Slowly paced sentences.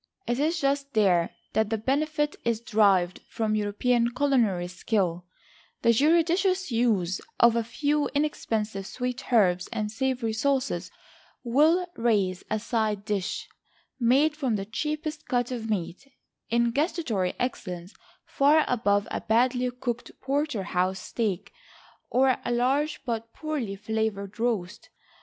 Yes: slow, 125 wpm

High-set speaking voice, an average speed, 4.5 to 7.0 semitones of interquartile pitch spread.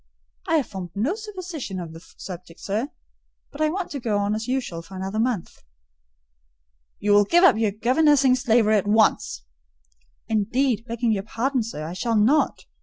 Yes: high, 225 Hz; average, 175 wpm; average, 4.9 semitones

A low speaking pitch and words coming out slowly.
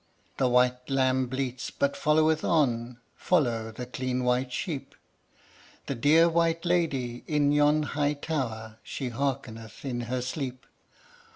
Yes: low, 130 Hz; slow, 130 wpm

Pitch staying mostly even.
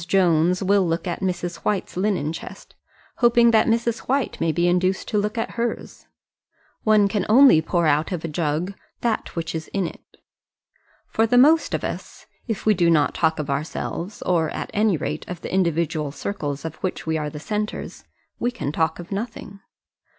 No: average, 4.7 semitones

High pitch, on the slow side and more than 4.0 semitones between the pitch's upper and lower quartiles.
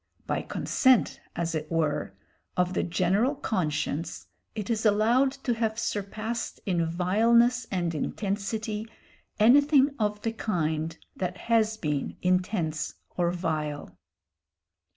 Yes: high, 200 Hz; slow, 115 wpm; average, 5.3 semitones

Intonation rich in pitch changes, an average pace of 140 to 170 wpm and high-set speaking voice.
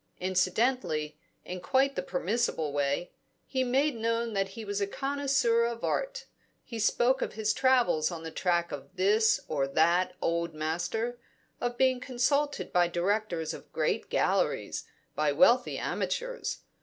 Yes: wide, 6.4 semitones; average, 145 wpm; high, 215 Hz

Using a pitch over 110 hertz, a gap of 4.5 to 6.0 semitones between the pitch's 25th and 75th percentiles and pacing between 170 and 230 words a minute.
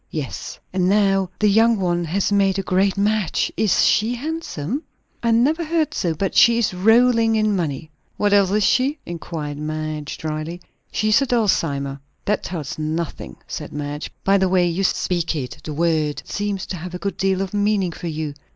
Yes: high, 190 Hz; average, 5.0 semitones; average, 190 wpm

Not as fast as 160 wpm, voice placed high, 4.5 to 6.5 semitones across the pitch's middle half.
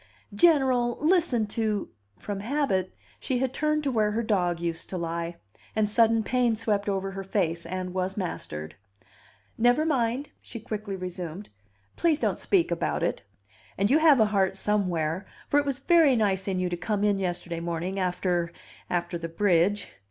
No: average, 175 wpm; high, 200 Hz; average, 5.1 semitones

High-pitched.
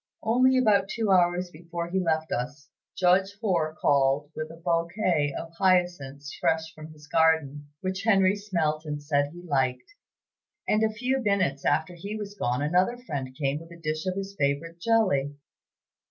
No: medium, 170 Hz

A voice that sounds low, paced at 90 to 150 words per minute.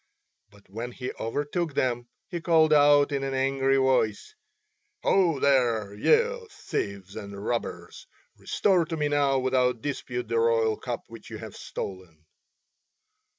Yes: low, 130 Hz; average, 140 wpm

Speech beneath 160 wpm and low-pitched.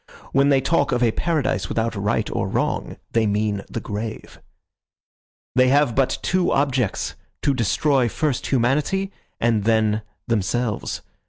Yes: average, 140 wpm; low, 120 Hz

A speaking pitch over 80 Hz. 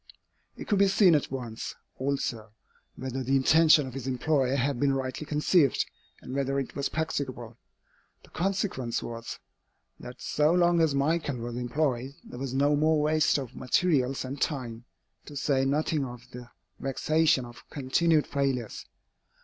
Yes: low, 135 Hz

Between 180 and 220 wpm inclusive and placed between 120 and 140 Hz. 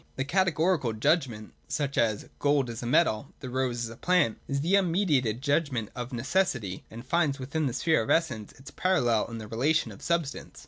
Yes: average, 200 wpm; low, 135 Hz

